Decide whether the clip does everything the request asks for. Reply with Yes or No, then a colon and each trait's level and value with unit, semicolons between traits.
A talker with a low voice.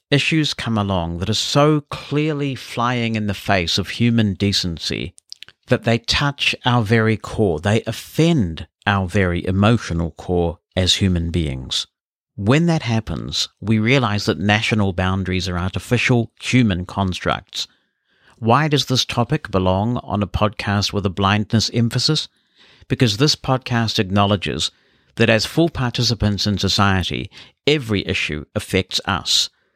Yes: low, 105 Hz